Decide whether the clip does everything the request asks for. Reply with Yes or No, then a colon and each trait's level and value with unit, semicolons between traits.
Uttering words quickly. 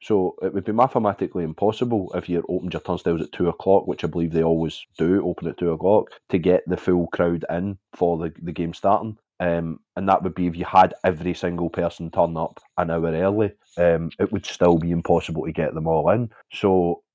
Yes: fast, 220 wpm